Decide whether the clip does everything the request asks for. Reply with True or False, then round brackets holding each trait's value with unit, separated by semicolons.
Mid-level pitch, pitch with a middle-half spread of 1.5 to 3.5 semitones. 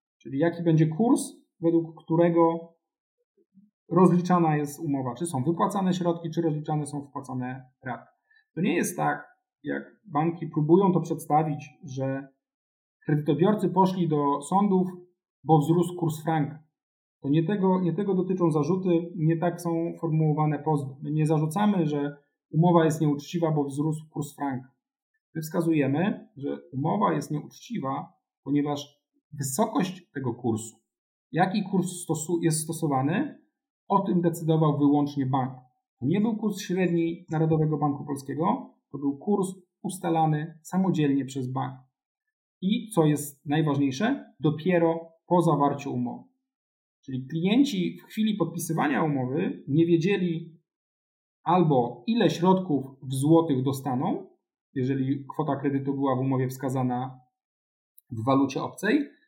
False (160 Hz; 4.0 semitones)